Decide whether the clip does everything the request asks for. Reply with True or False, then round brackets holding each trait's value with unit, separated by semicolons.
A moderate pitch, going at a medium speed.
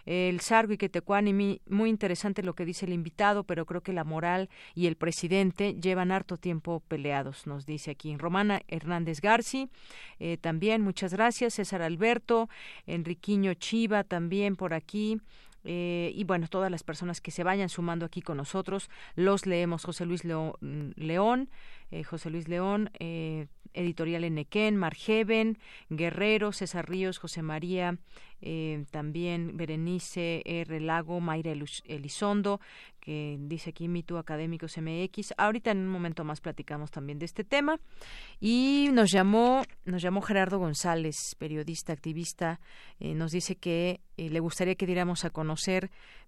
True (175 Hz; 150 wpm)